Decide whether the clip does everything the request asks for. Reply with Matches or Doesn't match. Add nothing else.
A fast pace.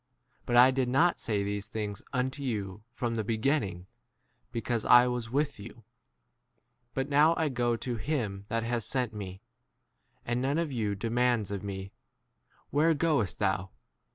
Doesn't match